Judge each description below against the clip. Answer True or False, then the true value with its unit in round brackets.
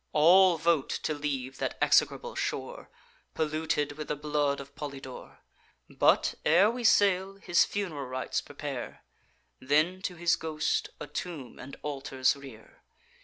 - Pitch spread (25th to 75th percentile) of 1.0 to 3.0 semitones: False (3.9 semitones)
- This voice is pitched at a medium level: True (150 Hz)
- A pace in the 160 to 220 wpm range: False (135 wpm)